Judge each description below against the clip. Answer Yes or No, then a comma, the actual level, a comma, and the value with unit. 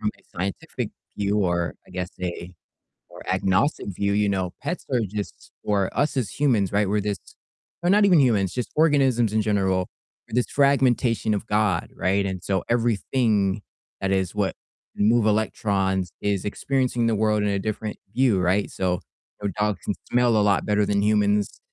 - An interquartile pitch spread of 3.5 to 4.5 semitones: No, average, 3.1 semitones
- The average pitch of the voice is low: Yes, low, 105 Hz